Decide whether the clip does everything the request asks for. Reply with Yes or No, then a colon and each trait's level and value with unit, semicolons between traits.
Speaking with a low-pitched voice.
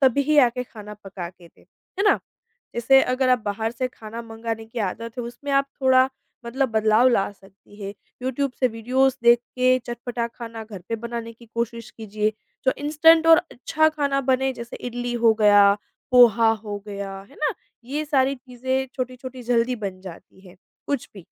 No: high, 240 Hz